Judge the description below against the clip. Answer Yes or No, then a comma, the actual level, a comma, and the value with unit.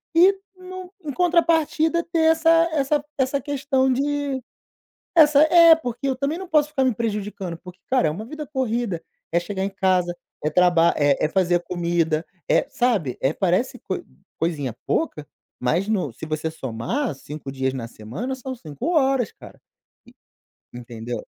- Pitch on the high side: Yes, high, 230 Hz